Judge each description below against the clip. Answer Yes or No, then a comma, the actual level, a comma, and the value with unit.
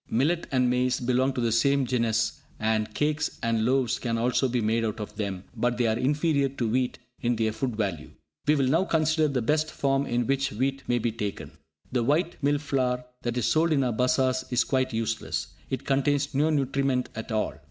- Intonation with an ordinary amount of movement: Yes, average, 3.2 semitones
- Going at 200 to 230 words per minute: Yes, fast, 205 wpm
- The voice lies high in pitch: No, low, 125 Hz